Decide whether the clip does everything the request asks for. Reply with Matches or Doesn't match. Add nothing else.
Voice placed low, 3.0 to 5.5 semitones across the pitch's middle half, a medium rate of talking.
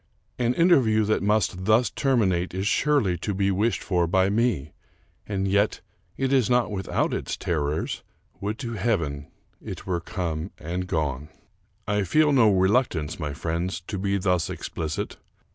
Matches